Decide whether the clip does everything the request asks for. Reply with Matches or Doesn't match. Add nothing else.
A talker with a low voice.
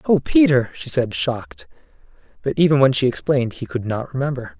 Matches